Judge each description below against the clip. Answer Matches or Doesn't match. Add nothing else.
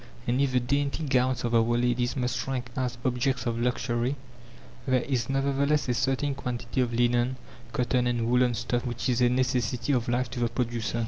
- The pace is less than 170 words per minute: Doesn't match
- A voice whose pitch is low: Matches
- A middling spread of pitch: Doesn't match